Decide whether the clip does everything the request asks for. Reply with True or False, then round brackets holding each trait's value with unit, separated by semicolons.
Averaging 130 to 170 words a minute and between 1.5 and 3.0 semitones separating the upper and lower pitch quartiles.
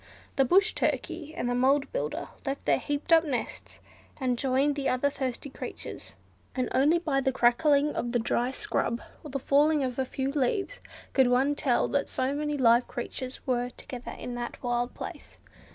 False (185 wpm; 2.7 semitones)